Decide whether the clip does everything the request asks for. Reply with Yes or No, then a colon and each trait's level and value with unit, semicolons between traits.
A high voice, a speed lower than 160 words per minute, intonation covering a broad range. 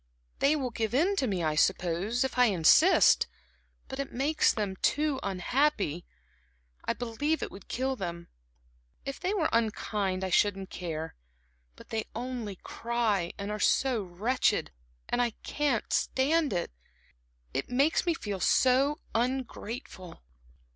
Yes: high, 235 Hz; average, 140 wpm; wide, 5.7 semitones